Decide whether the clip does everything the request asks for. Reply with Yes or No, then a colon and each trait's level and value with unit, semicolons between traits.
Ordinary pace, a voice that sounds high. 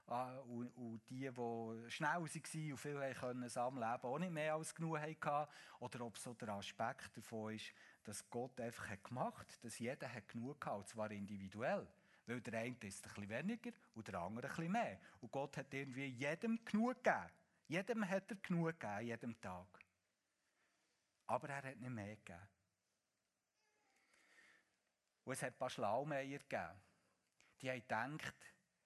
No: average, 165 wpm; low, 125 Hz